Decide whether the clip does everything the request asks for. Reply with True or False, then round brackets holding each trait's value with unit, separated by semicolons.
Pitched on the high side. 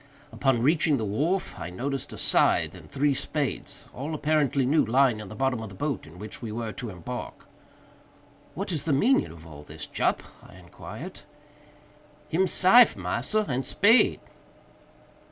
False (135 Hz)